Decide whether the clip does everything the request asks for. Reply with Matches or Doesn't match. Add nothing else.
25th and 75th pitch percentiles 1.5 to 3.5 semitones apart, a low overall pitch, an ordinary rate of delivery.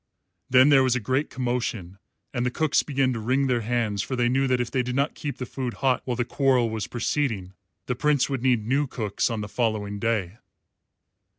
Doesn't match